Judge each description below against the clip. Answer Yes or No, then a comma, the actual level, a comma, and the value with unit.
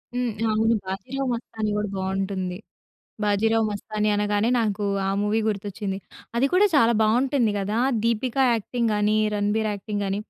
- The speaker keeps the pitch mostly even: Yes, narrow, 2.1 semitones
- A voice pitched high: Yes, high, 215 Hz